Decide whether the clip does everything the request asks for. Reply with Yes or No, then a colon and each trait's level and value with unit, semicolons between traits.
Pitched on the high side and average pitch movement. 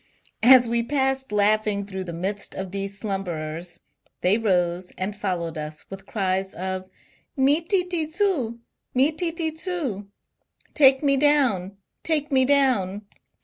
No: high, 210 Hz; wide, 6.8 semitones